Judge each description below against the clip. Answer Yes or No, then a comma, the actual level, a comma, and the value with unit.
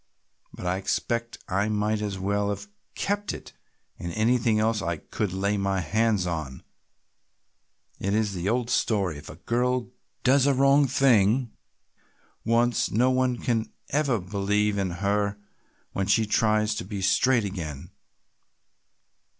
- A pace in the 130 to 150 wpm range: Yes, average, 140 wpm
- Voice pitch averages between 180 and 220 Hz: No, low, 105 Hz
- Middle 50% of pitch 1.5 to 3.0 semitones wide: No, average, 3.5 semitones